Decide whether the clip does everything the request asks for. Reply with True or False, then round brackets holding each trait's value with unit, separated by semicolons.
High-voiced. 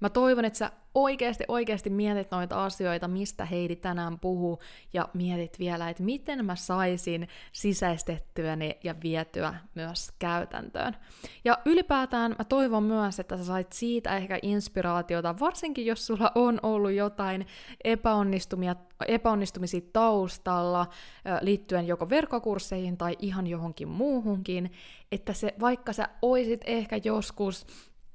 True (195 Hz)